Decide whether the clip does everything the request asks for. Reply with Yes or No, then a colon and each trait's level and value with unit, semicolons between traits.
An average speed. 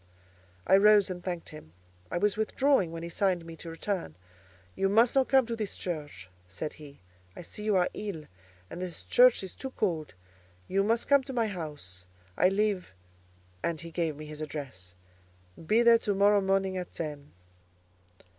Yes: average, 180 wpm